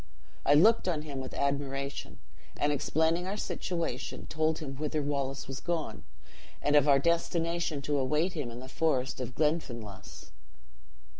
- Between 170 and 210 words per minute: No, average, 150 wpm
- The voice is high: No, medium, 145 Hz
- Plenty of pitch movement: No, average, 3.1 semitones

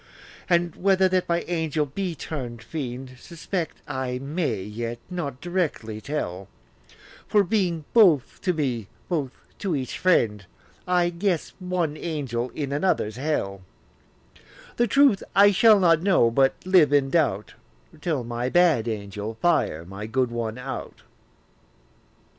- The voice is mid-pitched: Yes, medium, 150 Hz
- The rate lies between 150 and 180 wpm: No, slow, 135 wpm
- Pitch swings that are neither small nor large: No, wide, 6.9 semitones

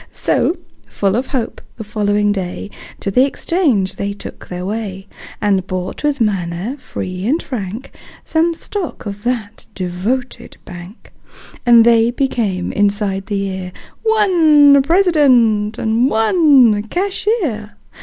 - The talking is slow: Yes, slow, 125 wpm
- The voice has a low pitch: No, high, 220 Hz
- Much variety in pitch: Yes, wide, 5.8 semitones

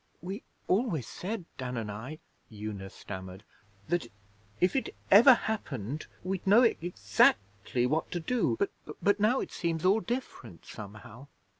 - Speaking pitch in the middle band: Yes, medium, 160 Hz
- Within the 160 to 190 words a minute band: No, average, 145 wpm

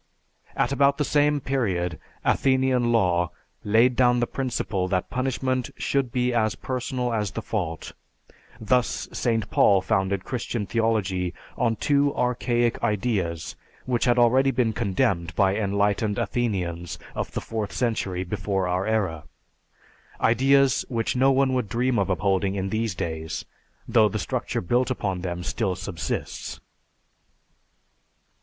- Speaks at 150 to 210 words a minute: No, slow, 135 wpm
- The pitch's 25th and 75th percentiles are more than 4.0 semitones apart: Yes, average, 4.7 semitones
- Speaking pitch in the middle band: No, low, 110 Hz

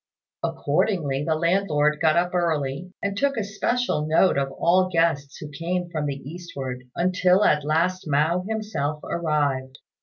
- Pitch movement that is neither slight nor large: Yes, average, 3.9 semitones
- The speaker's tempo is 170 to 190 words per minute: No, average, 145 wpm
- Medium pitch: Yes, medium, 165 Hz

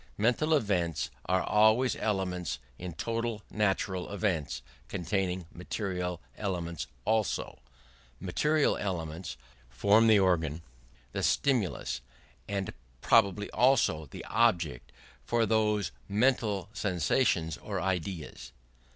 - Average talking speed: No, slow, 100 wpm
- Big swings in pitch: No, average, 3.9 semitones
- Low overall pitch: Yes, very low, 95 Hz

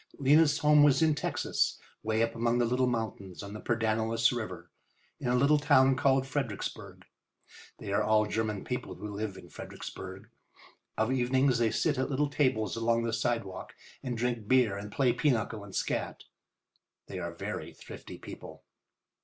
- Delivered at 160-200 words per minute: Yes, average, 165 wpm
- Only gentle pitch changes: No, average, 3.3 semitones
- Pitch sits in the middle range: No, low, 120 Hz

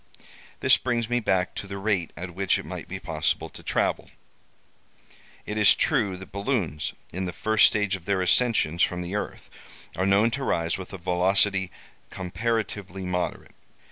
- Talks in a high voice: No, very low, 95 Hz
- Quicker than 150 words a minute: Yes, average, 170 wpm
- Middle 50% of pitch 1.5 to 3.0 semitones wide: Yes, narrow, 2.6 semitones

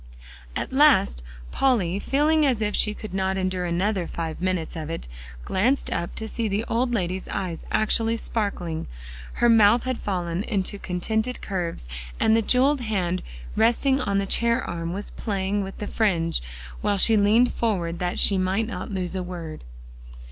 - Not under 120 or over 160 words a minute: No, average, 170 wpm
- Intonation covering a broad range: No, average, 4.1 semitones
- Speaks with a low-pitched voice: No, high, 200 Hz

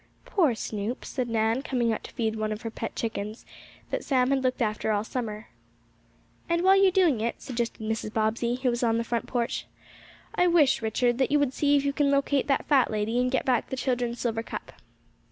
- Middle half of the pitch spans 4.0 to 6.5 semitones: No, average, 3.4 semitones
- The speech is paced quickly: Yes, fast, 220 wpm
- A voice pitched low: No, high, 240 Hz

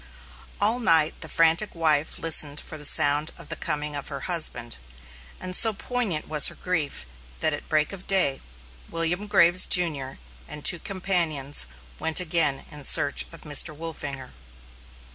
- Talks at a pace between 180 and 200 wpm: No, average, 155 wpm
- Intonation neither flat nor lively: Yes, average, 3.5 semitones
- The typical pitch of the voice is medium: Yes, medium, 160 Hz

